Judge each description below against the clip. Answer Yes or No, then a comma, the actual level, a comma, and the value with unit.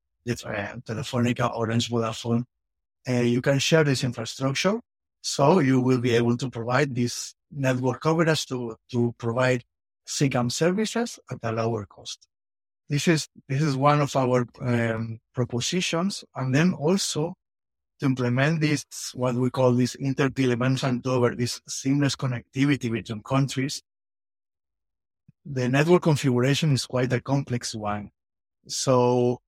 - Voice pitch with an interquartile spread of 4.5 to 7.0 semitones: No, average, 3.2 semitones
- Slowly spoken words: Yes, slow, 130 wpm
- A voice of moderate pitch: No, low, 125 Hz